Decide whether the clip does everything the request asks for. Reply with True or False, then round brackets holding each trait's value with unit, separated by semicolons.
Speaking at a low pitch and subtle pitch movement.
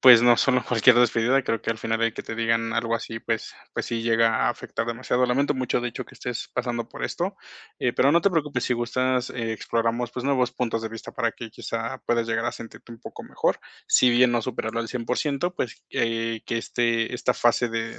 True (120 Hz; 1.6 semitones)